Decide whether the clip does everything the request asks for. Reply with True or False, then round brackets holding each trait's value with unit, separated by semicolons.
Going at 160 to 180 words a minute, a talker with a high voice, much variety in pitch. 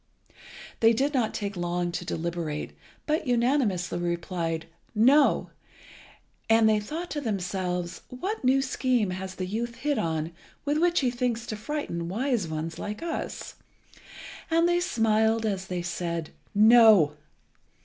False (140 wpm; 215 Hz; 6.5 semitones)